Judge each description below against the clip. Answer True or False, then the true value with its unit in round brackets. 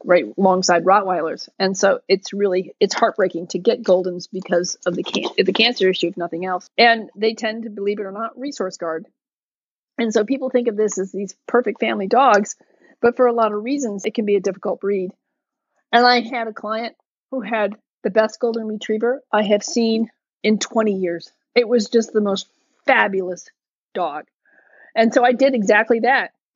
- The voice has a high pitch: True (220 Hz)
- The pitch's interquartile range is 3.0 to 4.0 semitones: True (3.7 semitones)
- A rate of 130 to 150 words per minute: False (190 wpm)